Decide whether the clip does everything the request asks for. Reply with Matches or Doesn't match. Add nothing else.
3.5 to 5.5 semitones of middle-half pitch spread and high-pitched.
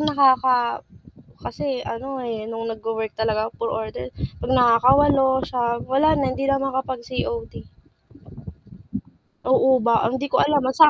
Doesn't match